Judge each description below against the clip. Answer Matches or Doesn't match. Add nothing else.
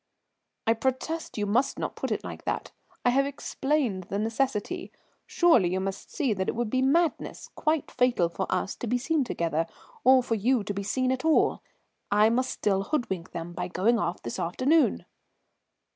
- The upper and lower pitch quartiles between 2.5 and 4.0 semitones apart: Doesn't match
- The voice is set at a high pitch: Matches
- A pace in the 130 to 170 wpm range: Doesn't match